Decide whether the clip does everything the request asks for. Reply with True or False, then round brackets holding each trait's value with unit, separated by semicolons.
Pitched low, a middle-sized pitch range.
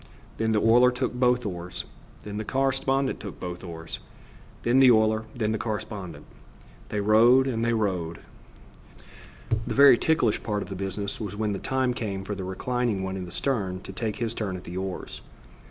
True (110 Hz; 4.2 semitones)